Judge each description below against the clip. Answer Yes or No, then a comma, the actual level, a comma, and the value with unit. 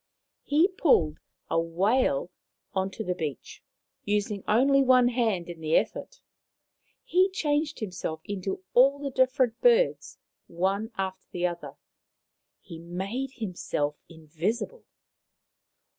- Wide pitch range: Yes, wide, 7.1 semitones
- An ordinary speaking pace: No, slow, 115 wpm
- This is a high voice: Yes, high, 210 Hz